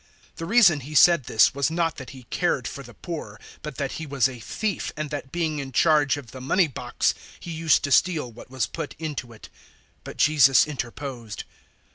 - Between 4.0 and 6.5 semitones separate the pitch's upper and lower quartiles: No, average, 3.6 semitones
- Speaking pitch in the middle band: Yes, medium, 145 Hz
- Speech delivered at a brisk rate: Yes, fast, 210 wpm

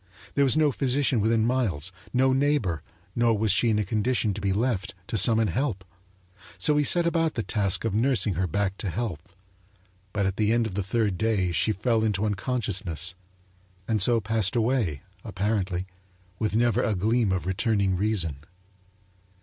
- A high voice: No, low, 110 Hz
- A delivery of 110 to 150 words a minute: No, average, 175 wpm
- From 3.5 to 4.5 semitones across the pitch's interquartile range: Yes, average, 3.8 semitones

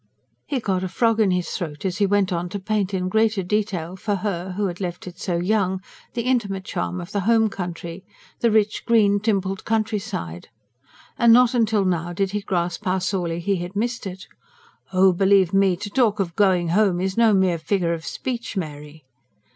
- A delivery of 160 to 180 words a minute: No, average, 195 wpm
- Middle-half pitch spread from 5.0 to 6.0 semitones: No, average, 3.1 semitones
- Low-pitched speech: No, high, 190 Hz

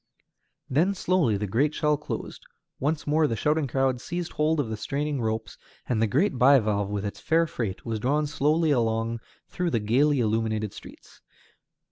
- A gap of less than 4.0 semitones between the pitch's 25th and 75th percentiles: No, average, 5.3 semitones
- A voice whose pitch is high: No, low, 135 Hz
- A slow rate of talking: No, average, 170 wpm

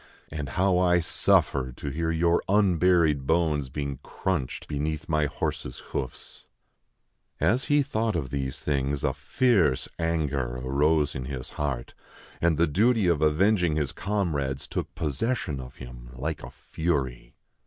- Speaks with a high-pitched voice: No, very low, 75 Hz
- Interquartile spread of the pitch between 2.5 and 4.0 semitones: No, average, 4.4 semitones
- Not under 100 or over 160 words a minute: Yes, average, 145 wpm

